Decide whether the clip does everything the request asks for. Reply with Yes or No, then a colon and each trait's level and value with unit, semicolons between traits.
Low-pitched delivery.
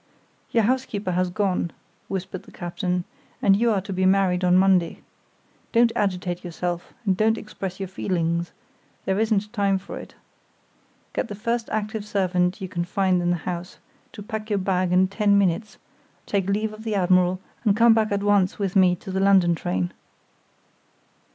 No: high, 190 Hz